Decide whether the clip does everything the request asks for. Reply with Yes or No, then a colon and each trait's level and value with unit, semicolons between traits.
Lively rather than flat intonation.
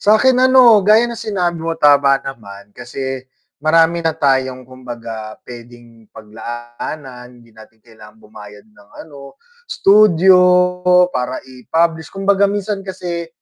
Yes: wide, 7.4 semitones